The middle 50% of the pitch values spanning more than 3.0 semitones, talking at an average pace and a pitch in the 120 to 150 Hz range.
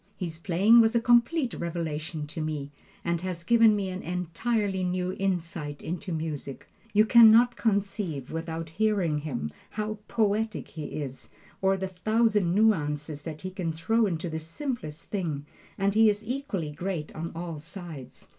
No: average, 5.0 semitones; average, 160 wpm; medium, 180 Hz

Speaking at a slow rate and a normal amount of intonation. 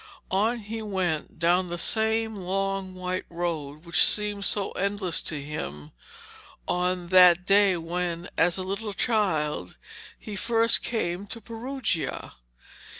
Yes: slow, 130 wpm; average, 3.4 semitones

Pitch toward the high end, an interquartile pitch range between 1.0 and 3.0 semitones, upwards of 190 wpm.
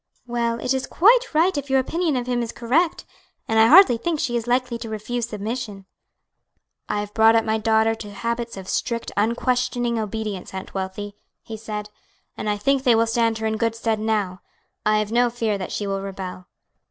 Yes: high, 225 Hz; narrow, 2.6 semitones; average, 200 wpm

